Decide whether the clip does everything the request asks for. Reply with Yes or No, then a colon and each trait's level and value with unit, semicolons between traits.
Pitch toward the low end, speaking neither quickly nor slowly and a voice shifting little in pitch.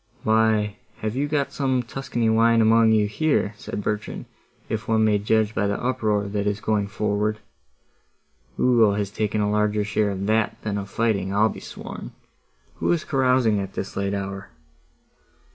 Yes: low, 105 Hz; average, 170 wpm; narrow, 1.6 semitones